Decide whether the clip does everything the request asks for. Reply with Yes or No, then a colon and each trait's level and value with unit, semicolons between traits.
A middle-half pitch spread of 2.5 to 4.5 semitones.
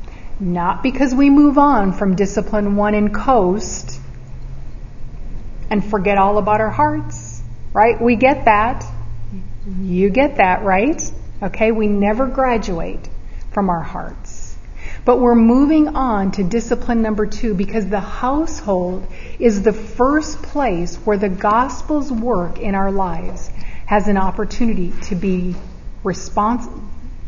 No: average, 5.2 semitones